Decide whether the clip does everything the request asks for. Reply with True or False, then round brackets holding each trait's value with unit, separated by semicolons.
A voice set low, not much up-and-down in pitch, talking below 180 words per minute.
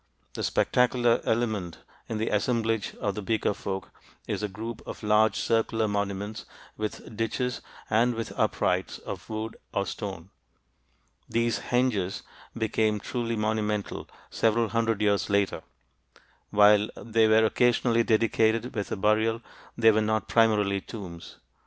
True (110 Hz; 1.8 semitones; 135 wpm)